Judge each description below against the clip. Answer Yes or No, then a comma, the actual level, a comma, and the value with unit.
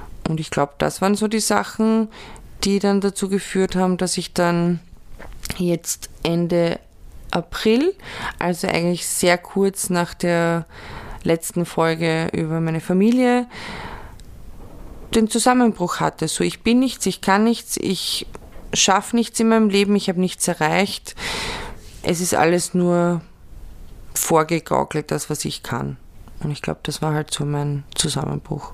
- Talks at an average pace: Yes, average, 140 wpm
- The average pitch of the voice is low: No, medium, 175 Hz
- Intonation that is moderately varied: Yes, average, 3.7 semitones